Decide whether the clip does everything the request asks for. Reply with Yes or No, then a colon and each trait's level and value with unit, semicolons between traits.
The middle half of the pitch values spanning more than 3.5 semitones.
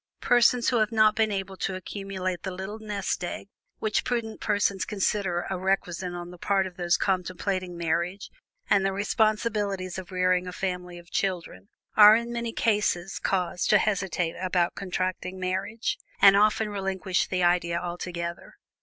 No: narrow, 2.5 semitones